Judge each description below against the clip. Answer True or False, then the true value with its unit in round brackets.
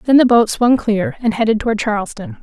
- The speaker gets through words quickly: True (225 wpm)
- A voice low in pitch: False (225 Hz)